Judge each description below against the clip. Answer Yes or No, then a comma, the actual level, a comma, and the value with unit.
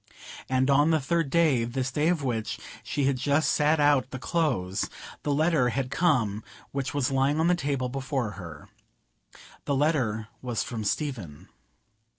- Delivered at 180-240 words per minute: No, average, 155 wpm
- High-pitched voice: No, low, 135 Hz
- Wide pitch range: No, average, 3.4 semitones